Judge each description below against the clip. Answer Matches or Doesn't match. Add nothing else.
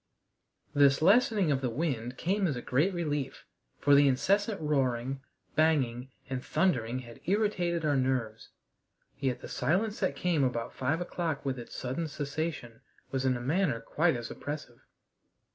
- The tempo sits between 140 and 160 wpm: Matches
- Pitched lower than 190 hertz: Matches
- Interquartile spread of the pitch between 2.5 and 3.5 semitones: Doesn't match